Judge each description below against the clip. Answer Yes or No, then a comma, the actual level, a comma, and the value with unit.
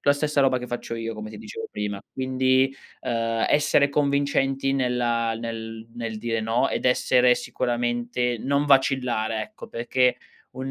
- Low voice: Yes, low, 125 Hz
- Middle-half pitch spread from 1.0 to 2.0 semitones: No, average, 2.7 semitones